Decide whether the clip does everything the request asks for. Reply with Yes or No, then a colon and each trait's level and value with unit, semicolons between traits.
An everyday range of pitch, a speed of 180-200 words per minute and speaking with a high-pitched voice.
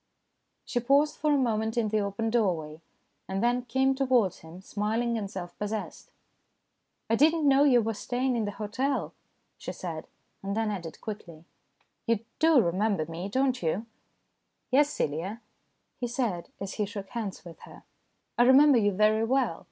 Yes: average, 4.4 semitones; average, 185 wpm; high, 220 Hz